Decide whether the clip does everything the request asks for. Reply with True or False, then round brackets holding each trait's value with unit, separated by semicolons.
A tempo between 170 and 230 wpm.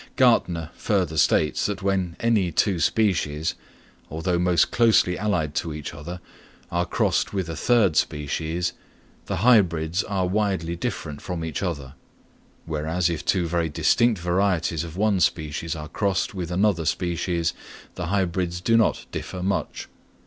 False (145 wpm)